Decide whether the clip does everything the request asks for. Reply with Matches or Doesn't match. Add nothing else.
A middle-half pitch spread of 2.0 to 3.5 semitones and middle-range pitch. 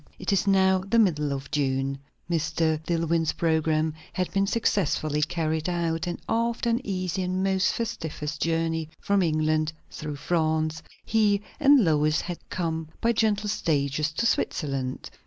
Doesn't match